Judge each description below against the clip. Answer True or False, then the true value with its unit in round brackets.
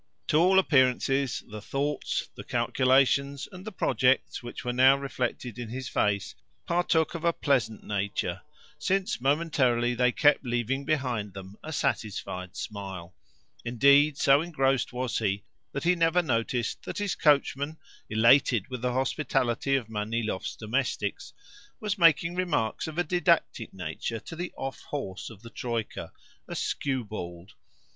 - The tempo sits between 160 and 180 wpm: False (145 wpm)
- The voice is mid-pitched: False (130 Hz)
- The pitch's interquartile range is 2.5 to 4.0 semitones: False (4.7 semitones)